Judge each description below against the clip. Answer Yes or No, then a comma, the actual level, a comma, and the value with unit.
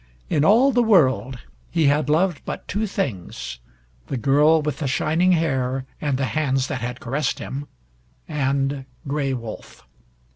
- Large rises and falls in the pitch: No, average, 3.3 semitones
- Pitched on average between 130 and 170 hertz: Yes, medium, 140 Hz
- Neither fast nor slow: Yes, average, 150 wpm